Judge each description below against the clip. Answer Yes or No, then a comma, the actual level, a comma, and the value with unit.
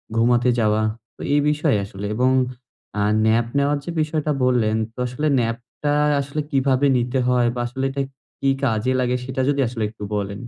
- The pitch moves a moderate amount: Yes, average, 3.4 semitones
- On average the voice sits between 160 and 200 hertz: No, low, 125 Hz